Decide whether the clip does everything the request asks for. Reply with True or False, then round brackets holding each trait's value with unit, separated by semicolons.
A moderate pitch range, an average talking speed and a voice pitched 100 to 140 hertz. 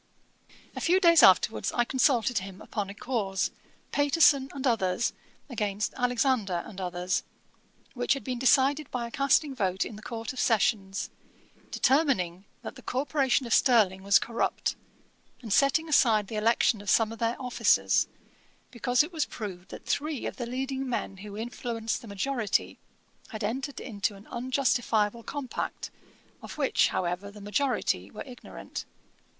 False (4.6 semitones; 155 wpm; 235 Hz)